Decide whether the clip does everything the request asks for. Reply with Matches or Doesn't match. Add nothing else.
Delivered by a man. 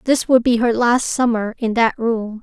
Doesn't match